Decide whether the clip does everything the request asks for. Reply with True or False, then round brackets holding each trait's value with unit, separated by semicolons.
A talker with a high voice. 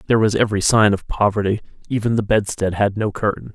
False (105 Hz)